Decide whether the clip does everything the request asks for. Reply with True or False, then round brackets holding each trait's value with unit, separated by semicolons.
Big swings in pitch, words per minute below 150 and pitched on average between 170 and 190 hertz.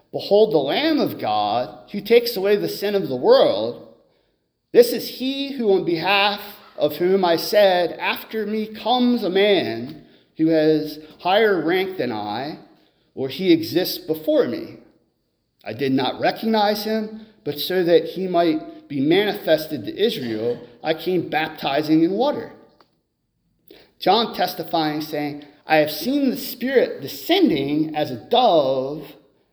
True (7.3 semitones; 140 wpm; 185 Hz)